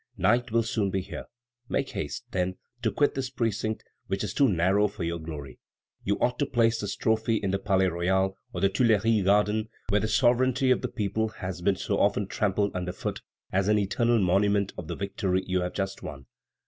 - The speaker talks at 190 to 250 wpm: Yes, fast, 205 wpm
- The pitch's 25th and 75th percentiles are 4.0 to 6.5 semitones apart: No, average, 2.9 semitones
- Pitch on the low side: Yes, low, 100 Hz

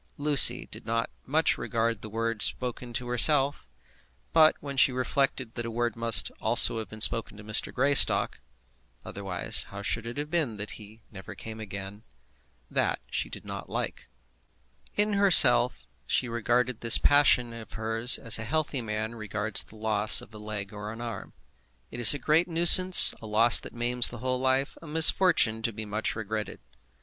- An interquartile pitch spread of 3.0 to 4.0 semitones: Yes, average, 3.5 semitones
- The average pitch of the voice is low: Yes, low, 115 Hz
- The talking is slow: No, average, 180 wpm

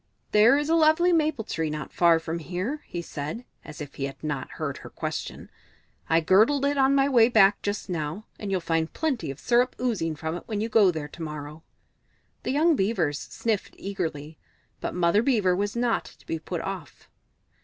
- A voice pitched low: No, high, 195 Hz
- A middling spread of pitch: No, wide, 7.0 semitones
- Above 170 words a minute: Yes, average, 195 wpm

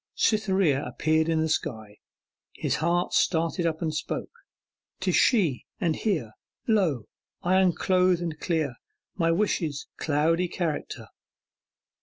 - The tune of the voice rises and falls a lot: No, average, 2.8 semitones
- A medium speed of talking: No, slow, 120 wpm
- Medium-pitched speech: Yes, medium, 165 Hz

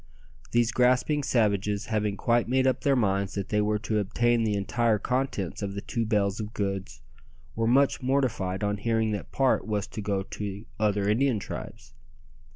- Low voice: Yes, low, 105 Hz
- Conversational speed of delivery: Yes, average, 175 wpm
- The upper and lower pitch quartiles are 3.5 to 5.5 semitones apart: No, average, 2.9 semitones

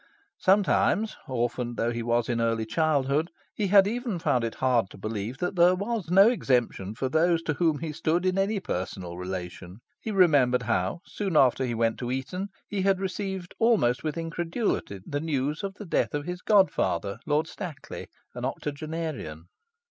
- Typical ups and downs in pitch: No, wide, 7.7 semitones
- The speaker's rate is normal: Yes, average, 175 wpm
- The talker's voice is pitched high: No, medium, 155 Hz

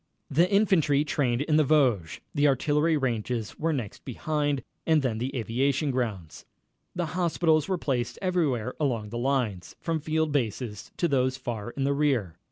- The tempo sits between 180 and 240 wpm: No, average, 165 wpm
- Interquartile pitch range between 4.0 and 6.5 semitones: Yes, average, 4.5 semitones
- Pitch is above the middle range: No, low, 135 Hz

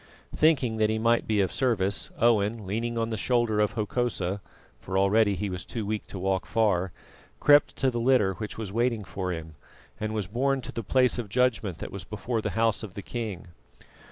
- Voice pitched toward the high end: No, low, 110 Hz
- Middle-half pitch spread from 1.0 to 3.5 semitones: Yes, average, 3.2 semitones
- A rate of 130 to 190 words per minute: No, fast, 205 wpm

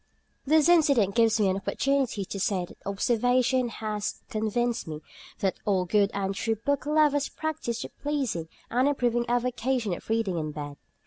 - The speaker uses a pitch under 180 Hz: No, high, 230 Hz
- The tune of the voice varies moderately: Yes, average, 4.8 semitones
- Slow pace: No, average, 165 wpm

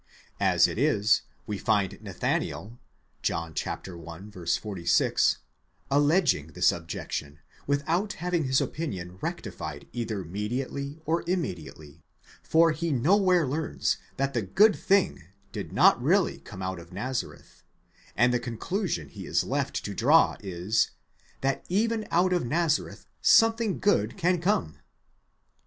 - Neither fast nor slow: No, slow, 125 wpm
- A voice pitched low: Yes, low, 125 Hz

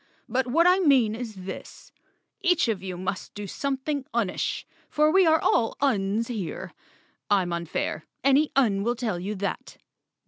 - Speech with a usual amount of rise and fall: No, wide, 6.0 semitones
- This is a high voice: Yes, high, 230 Hz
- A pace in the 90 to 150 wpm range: No, average, 160 wpm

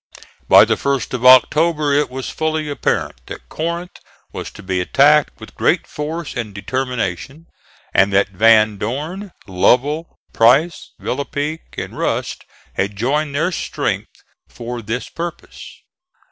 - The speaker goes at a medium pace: No, slow, 130 wpm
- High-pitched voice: No, low, 135 Hz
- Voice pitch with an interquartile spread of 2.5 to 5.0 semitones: No, wide, 5.5 semitones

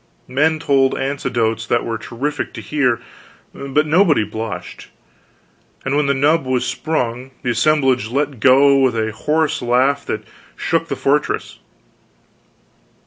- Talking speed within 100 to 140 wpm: Yes, slow, 135 wpm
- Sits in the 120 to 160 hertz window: Yes, low, 135 Hz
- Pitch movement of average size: Yes, average, 3.7 semitones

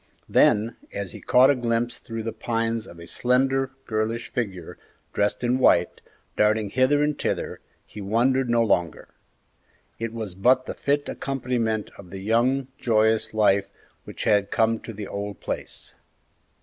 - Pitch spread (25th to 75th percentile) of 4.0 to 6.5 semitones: No, average, 3.4 semitones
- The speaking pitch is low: Yes, low, 115 Hz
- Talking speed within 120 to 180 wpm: Yes, average, 155 wpm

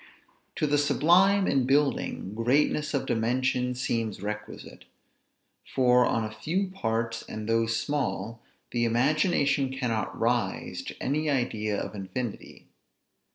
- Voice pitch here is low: Yes, low, 125 Hz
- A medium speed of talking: No, slow, 120 wpm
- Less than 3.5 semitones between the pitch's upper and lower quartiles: No, average, 4.2 semitones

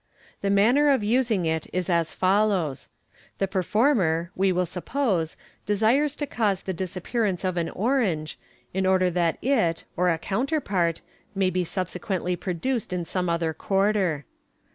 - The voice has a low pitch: No, medium, 185 Hz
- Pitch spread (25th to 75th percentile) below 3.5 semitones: No, average, 3.8 semitones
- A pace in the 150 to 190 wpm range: Yes, average, 160 wpm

